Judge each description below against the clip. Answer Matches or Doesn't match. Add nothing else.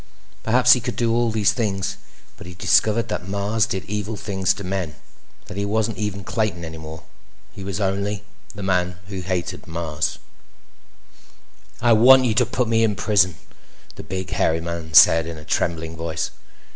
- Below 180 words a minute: Doesn't match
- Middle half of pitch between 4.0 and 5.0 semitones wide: Matches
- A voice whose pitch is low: Matches